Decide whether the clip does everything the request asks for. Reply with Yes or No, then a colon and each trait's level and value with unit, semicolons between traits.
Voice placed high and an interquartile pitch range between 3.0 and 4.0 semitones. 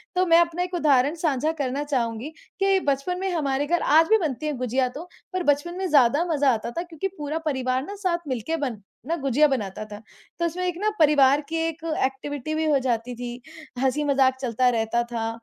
No: very high, 290 Hz; average, 4.6 semitones